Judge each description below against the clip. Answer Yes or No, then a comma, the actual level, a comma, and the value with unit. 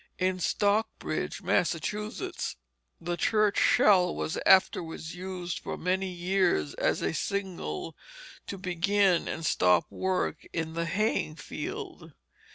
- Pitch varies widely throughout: No, average, 2.9 semitones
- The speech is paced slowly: Yes, slow, 115 wpm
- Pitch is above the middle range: No, medium, 180 Hz